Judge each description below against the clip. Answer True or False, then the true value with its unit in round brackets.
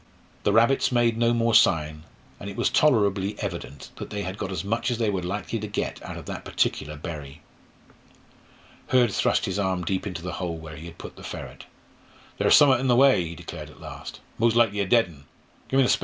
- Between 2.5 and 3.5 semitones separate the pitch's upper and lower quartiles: False (5.1 semitones)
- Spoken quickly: True (210 wpm)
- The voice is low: True (100 Hz)